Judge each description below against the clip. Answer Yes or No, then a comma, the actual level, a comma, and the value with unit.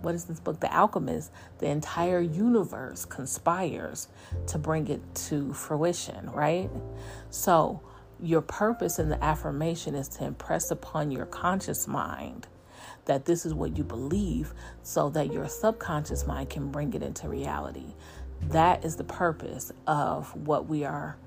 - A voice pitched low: No, medium, 145 Hz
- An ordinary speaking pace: Yes, average, 150 wpm